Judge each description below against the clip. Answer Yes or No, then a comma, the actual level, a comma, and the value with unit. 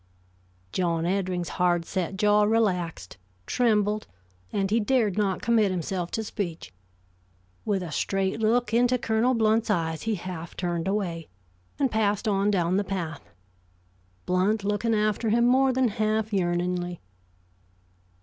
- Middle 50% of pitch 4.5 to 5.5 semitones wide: No, average, 3.7 semitones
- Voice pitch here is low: No, high, 200 Hz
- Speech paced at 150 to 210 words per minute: No, slow, 135 wpm